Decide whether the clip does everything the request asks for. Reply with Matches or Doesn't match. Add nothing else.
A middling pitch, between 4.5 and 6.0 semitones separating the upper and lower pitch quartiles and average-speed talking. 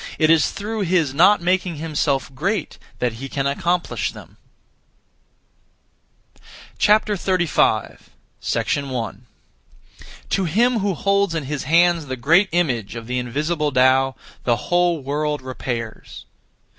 Doesn't match